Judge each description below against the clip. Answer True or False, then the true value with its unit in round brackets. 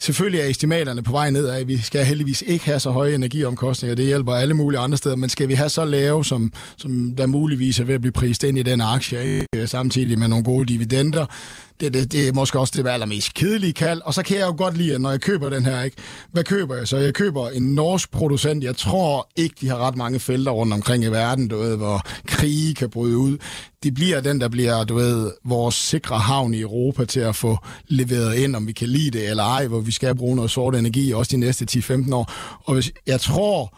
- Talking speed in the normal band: False (250 wpm)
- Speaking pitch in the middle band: False (130 Hz)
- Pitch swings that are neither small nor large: True (3.0 semitones)